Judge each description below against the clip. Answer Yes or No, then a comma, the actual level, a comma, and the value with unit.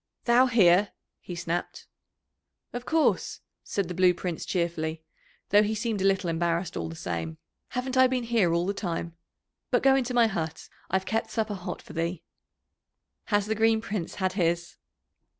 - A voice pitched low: No, high, 190 Hz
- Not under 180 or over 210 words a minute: No, average, 170 wpm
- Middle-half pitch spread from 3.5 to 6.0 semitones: Yes, average, 4.6 semitones